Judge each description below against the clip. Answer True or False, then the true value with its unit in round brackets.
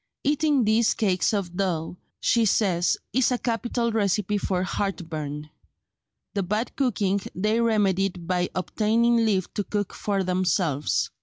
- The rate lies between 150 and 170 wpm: False (135 wpm)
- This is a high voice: True (200 Hz)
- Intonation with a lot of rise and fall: False (3.7 semitones)